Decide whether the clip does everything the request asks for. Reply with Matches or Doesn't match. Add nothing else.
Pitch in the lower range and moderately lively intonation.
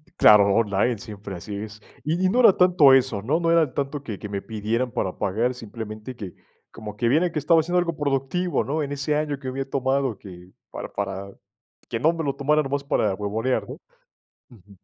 Doesn't match